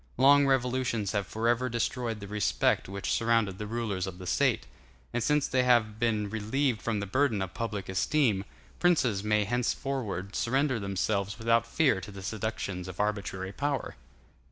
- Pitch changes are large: No, average, 4.0 semitones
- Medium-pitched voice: No, low, 110 Hz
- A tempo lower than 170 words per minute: Yes, average, 160 wpm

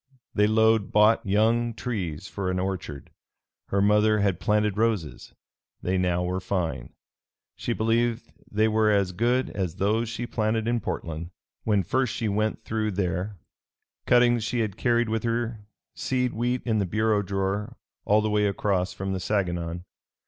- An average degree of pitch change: Yes, average, 3.0 semitones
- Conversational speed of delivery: Yes, average, 160 wpm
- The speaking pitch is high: No, low, 105 Hz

